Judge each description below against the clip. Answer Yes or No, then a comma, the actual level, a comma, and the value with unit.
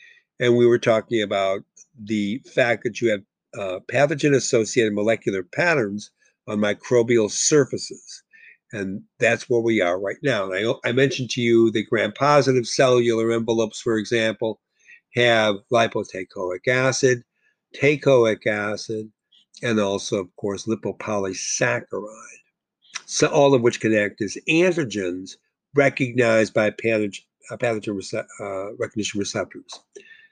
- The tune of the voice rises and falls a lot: No, average, 4.4 semitones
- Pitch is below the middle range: Yes, low, 115 Hz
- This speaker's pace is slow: Yes, slow, 115 wpm